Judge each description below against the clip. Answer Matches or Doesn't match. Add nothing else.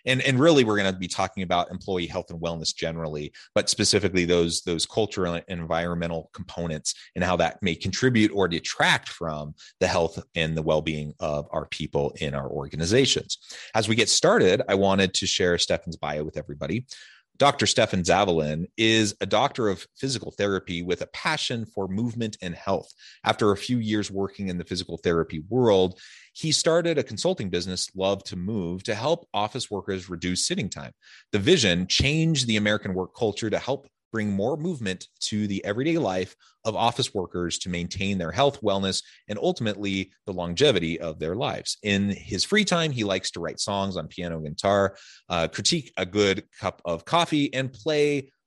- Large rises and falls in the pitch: Doesn't match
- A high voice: Doesn't match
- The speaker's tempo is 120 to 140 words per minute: Doesn't match